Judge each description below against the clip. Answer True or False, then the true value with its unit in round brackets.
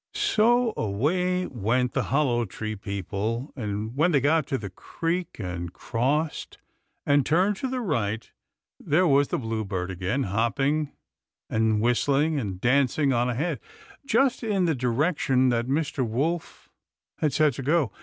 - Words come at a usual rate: True (145 wpm)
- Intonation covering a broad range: True (6.0 semitones)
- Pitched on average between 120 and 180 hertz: True (135 Hz)